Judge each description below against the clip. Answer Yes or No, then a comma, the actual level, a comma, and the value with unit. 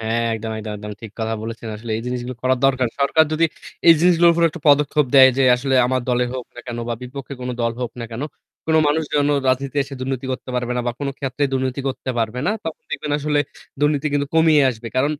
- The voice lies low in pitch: Yes, low, 130 Hz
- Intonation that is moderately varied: Yes, average, 3.3 semitones